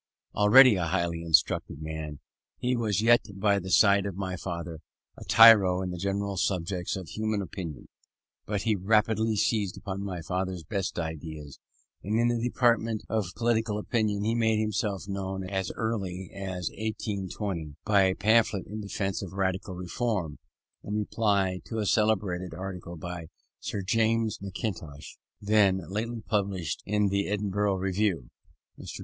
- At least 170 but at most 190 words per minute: No, average, 150 wpm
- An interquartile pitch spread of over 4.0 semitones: No, average, 2.9 semitones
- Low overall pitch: Yes, low, 100 Hz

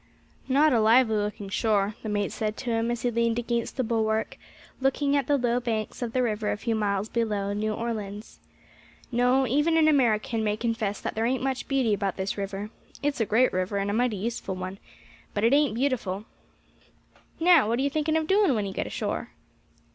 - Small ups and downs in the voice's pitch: No, average, 3.6 semitones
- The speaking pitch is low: No, high, 230 Hz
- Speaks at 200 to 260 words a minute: Yes, fast, 205 wpm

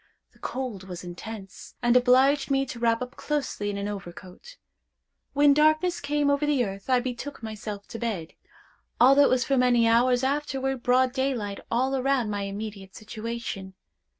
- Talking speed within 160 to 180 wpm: Yes, average, 165 wpm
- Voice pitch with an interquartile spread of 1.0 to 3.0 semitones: No, average, 4.6 semitones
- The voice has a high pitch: Yes, high, 245 Hz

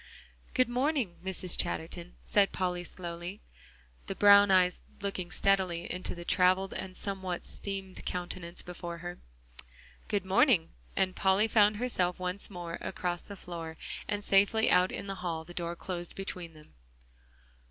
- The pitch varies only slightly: Yes, narrow, 2.3 semitones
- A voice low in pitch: No, medium, 185 Hz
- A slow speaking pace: No, average, 145 wpm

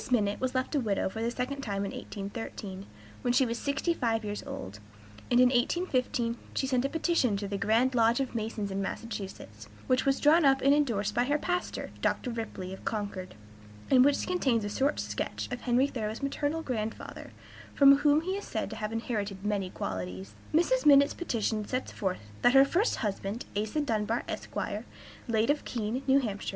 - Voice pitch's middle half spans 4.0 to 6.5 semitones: Yes, average, 4.8 semitones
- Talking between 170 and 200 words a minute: Yes, average, 190 wpm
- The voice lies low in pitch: No, high, 235 Hz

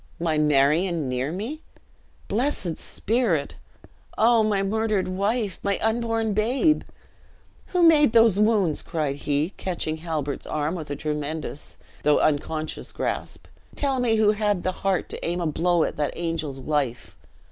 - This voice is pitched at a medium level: Yes, medium, 180 Hz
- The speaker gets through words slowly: No, average, 145 wpm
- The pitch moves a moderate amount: No, wide, 6.3 semitones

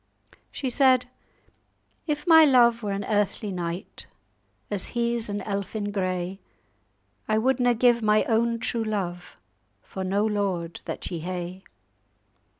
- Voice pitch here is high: Yes, high, 210 Hz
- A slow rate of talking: Yes, slow, 130 wpm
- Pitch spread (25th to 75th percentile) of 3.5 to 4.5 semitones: Yes, average, 3.8 semitones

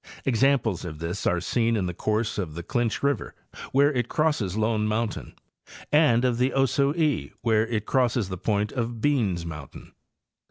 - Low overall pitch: Yes, low, 115 Hz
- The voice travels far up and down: No, average, 4.6 semitones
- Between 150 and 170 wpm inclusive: Yes, average, 165 wpm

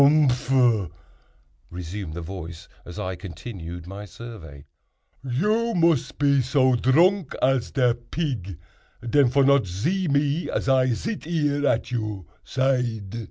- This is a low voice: Yes, low, 125 Hz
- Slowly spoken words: Yes, slow, 130 wpm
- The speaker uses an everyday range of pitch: No, wide, 6.6 semitones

